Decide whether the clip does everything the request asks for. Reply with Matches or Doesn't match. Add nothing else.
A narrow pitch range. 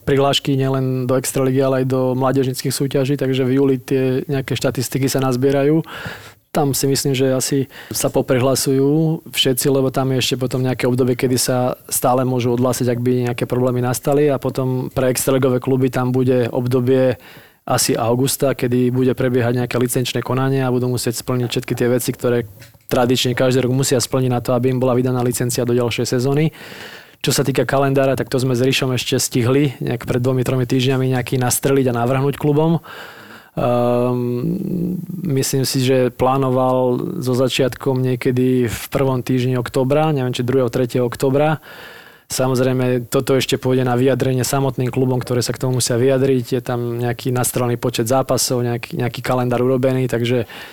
Matches